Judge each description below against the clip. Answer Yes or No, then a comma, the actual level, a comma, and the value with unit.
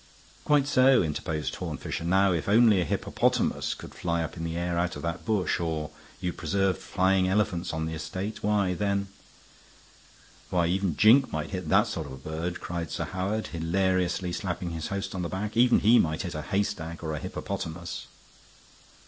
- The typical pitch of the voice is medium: No, very low, 90 Hz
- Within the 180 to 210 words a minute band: Yes, average, 185 wpm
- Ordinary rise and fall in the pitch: Yes, average, 3.2 semitones